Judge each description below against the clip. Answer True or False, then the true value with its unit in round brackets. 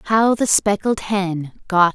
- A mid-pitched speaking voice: False (200 Hz)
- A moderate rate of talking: True (155 wpm)